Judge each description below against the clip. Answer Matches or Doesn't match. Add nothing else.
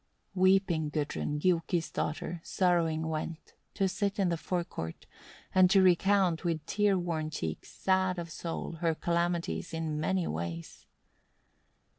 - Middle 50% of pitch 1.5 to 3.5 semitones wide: Matches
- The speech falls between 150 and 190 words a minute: Doesn't match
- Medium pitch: Matches